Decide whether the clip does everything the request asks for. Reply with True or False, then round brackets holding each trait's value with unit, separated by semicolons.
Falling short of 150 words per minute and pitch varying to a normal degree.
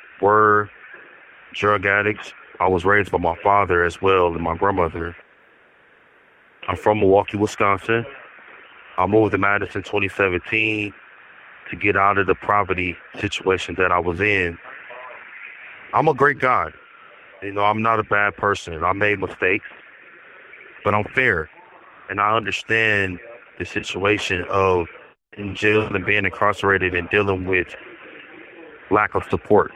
False (135 wpm; 2.2 semitones)